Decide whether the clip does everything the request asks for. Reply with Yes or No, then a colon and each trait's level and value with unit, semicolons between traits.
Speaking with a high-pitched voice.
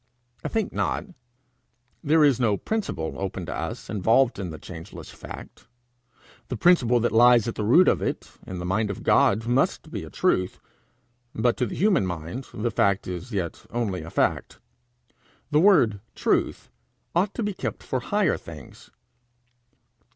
No: low, 115 Hz